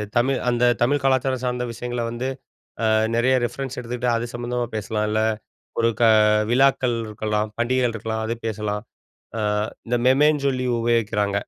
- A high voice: No, low, 120 Hz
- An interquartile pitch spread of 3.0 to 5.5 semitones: No, narrow, 2.5 semitones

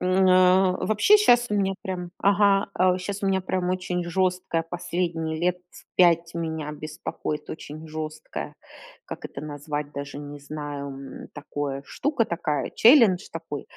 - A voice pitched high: No, medium, 170 Hz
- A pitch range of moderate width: Yes, average, 3.7 semitones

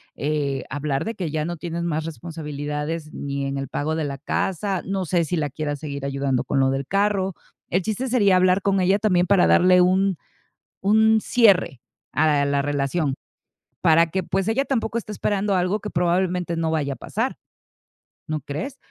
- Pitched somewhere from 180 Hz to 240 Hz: No, medium, 170 Hz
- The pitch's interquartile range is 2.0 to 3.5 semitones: No, average, 4.8 semitones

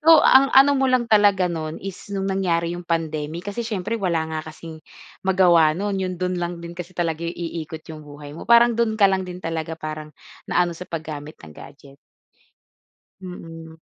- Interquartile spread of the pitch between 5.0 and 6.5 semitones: No, average, 3.3 semitones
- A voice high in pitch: No, medium, 175 Hz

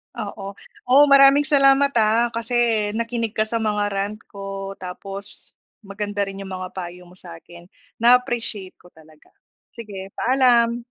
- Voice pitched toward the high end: Yes, high, 210 Hz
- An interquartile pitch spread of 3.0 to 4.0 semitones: Yes, average, 3.4 semitones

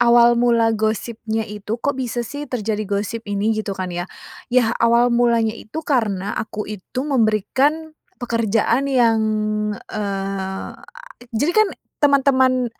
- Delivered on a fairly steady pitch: No, average, 3.0 semitones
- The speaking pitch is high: Yes, high, 230 Hz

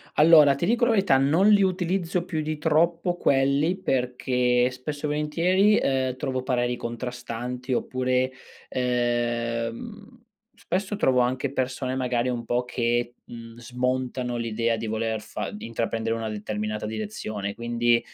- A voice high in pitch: No, low, 125 Hz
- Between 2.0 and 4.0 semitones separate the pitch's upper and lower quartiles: No, average, 4.4 semitones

